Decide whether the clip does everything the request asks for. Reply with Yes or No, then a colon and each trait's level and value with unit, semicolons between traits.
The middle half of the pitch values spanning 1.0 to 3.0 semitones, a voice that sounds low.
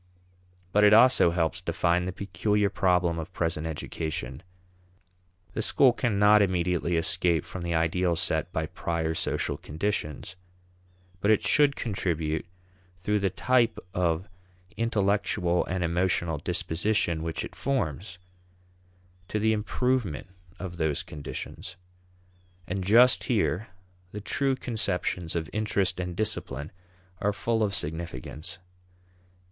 No: average, 4.2 semitones; very low, 90 Hz